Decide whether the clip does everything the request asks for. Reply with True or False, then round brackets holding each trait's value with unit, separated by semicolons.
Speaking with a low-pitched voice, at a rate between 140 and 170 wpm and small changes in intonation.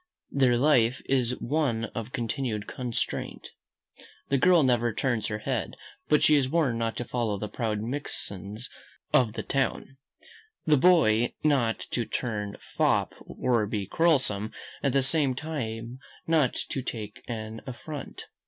False (125 Hz; 145 wpm; 3.8 semitones)